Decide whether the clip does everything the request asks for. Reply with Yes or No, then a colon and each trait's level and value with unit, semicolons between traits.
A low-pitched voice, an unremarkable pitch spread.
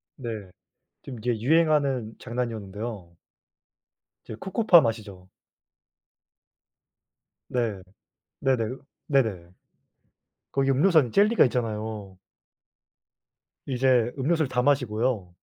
Yes: low, 120 Hz; average, 4.1 semitones